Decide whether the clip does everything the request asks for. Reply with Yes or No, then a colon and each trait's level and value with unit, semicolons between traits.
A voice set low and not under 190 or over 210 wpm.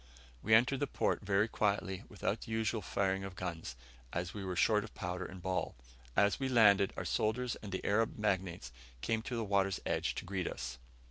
Yes: low, 100 Hz; average, 200 wpm